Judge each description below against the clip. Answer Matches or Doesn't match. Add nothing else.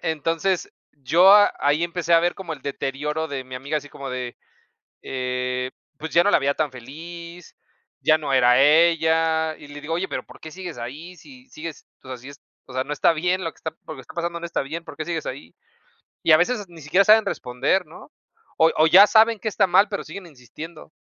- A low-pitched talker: Doesn't match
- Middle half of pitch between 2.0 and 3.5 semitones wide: Doesn't match